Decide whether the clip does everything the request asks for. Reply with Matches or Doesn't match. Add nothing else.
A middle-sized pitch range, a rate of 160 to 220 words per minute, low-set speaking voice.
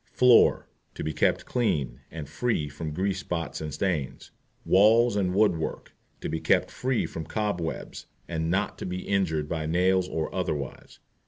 Matches